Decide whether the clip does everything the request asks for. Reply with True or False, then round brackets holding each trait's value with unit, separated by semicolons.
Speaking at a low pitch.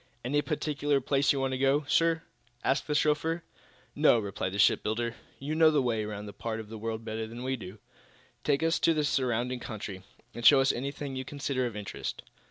True (130 Hz)